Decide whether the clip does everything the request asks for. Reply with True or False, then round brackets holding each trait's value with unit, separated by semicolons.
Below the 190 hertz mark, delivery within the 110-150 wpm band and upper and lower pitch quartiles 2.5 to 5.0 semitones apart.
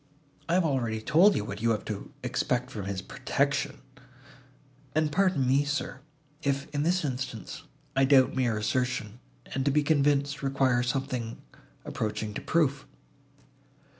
True (135 Hz; 145 wpm; 3.7 semitones)